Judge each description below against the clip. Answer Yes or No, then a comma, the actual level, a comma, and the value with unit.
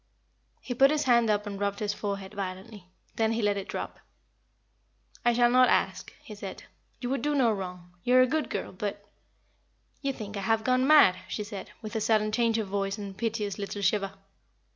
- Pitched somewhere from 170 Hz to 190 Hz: No, high, 215 Hz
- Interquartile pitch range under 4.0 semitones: Yes, average, 3.2 semitones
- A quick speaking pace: Yes, fast, 210 wpm